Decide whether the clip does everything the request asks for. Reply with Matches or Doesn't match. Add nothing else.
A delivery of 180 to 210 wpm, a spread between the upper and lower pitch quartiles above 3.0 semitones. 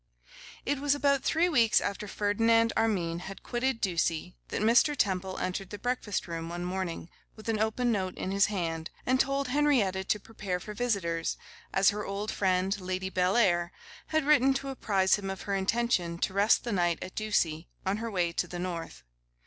Matches